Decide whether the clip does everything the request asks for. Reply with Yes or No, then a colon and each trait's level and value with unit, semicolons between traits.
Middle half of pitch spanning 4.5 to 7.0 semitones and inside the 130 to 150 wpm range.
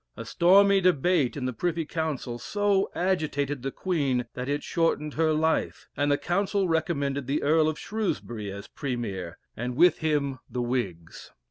No: average, 5.2 semitones; average, 160 wpm